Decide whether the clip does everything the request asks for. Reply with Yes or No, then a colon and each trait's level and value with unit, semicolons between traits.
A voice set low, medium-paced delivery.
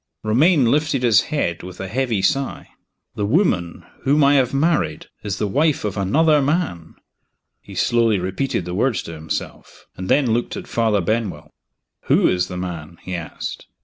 Yes: low, 110 Hz; average, 170 wpm